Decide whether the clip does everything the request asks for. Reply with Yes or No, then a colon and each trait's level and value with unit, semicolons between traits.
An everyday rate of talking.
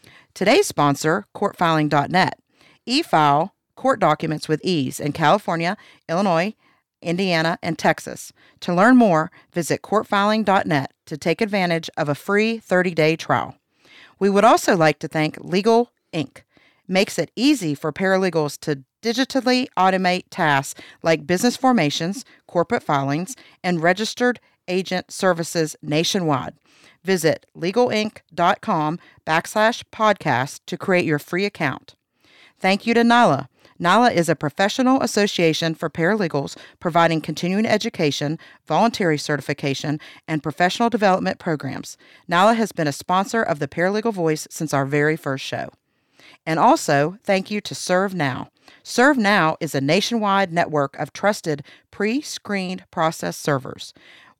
No: slow, 120 wpm